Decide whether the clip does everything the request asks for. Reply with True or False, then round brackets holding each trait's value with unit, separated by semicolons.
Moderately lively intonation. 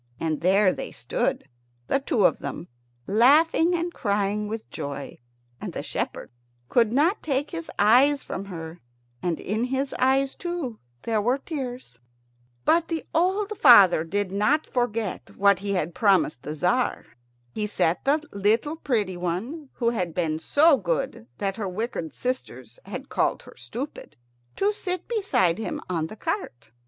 False (7.5 semitones)